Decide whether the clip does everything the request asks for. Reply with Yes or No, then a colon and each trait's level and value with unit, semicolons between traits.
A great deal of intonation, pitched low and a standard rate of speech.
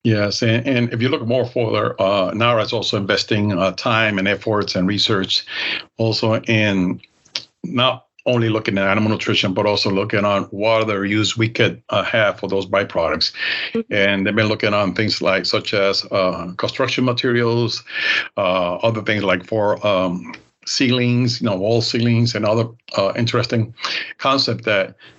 No: average, 2.8 semitones; low, 110 Hz; average, 165 wpm